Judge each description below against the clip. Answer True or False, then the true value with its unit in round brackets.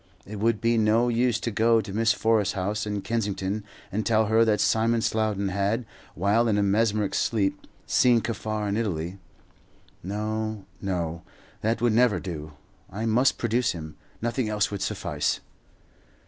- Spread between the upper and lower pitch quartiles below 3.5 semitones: True (2.4 semitones)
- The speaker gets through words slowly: False (160 wpm)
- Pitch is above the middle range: False (110 Hz)